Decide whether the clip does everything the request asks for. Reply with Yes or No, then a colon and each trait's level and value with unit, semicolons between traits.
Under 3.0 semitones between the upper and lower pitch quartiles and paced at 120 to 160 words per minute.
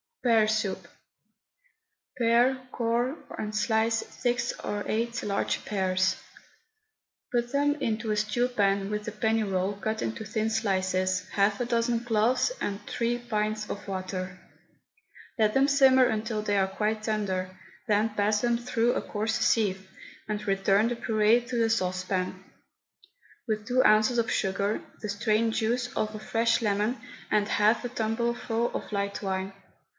Yes: narrow, 2.6 semitones; average, 150 wpm